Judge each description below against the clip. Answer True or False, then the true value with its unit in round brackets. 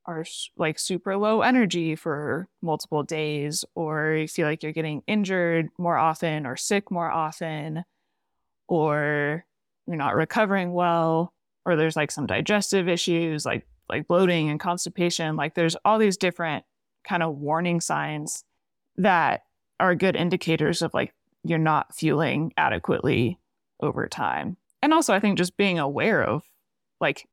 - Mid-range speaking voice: True (165 Hz)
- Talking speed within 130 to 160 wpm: True (145 wpm)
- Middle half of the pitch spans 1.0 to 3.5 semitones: True (2.7 semitones)